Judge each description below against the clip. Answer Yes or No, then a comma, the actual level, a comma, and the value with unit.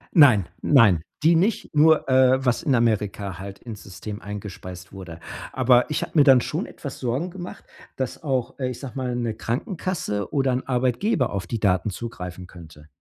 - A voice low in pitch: Yes, low, 120 Hz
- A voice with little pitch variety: No, average, 5.3 semitones